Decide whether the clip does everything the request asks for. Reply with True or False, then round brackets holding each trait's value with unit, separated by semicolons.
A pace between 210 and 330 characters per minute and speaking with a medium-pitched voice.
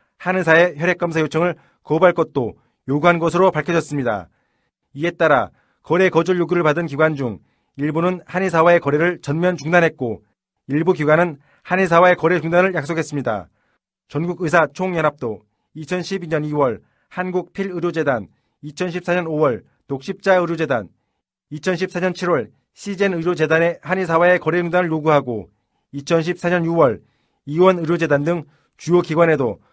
True (295 characters per minute; 170 Hz)